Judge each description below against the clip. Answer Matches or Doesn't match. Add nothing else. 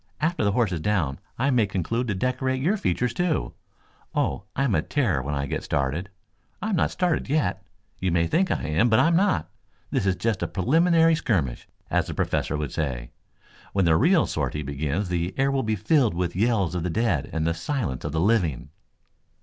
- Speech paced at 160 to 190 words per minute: Doesn't match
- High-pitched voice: Doesn't match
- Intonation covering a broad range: Matches